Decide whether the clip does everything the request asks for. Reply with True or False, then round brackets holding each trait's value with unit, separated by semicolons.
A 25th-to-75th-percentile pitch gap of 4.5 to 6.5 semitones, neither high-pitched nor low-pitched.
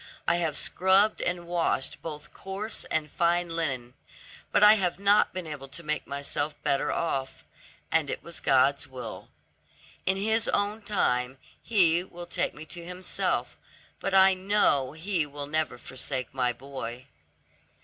True (5.1 semitones; 170 Hz)